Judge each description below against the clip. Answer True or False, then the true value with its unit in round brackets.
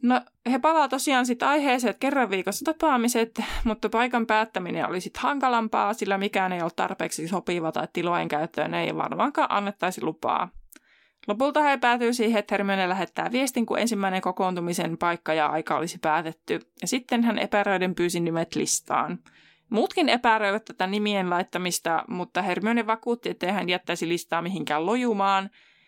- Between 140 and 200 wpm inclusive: True (155 wpm)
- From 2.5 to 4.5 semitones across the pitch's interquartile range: False (5.1 semitones)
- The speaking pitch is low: False (200 Hz)